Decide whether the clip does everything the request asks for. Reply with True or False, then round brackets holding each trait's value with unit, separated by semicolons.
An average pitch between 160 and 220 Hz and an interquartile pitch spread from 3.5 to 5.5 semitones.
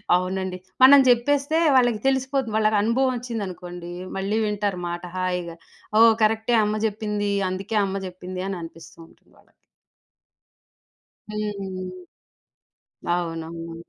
True (205 Hz; 3.9 semitones)